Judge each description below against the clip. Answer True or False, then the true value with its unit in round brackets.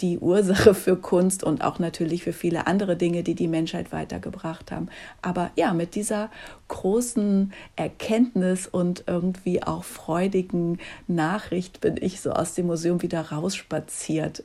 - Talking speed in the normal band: True (145 wpm)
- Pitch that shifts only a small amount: True (2.2 semitones)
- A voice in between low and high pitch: True (180 Hz)